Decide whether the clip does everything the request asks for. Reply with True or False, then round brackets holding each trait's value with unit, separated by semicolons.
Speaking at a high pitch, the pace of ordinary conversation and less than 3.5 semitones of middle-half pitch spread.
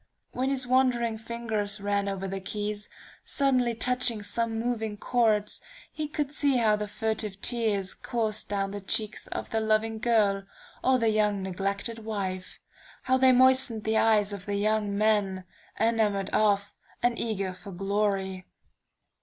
True (215 Hz; 150 wpm; 2.6 semitones)